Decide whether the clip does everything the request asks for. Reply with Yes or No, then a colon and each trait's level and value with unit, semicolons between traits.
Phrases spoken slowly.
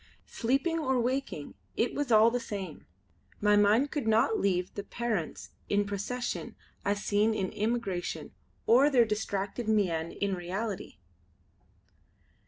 Yes: slow, 130 wpm